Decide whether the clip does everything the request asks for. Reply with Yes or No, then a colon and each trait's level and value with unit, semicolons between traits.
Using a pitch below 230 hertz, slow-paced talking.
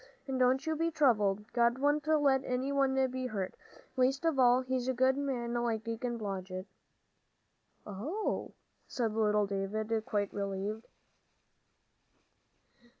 No: high, 245 Hz; slow, 125 wpm